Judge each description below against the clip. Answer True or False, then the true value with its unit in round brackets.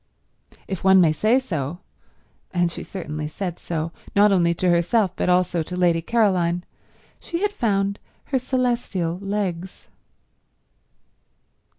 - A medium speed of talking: False (125 wpm)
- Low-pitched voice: False (185 Hz)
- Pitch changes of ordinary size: True (3.4 semitones)